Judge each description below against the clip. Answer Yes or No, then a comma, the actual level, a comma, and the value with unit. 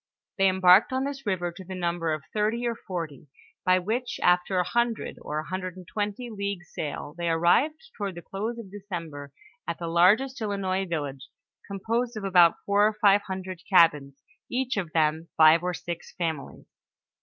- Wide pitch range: No, average, 3.7 semitones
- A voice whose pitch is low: No, medium, 185 Hz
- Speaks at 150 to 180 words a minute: Yes, average, 175 wpm